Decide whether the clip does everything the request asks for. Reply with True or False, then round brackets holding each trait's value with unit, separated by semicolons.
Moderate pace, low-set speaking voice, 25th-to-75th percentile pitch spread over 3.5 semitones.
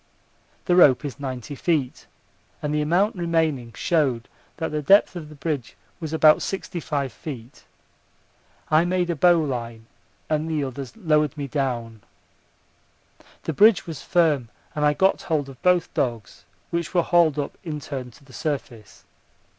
False (155 wpm; 150 Hz; 4.0 semitones)